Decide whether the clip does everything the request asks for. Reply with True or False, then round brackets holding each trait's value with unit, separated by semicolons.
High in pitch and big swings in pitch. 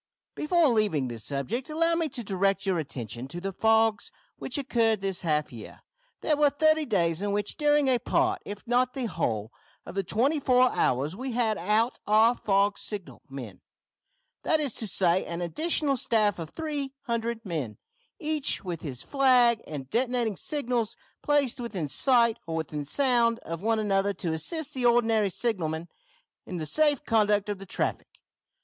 True (220 Hz; 6.6 semitones)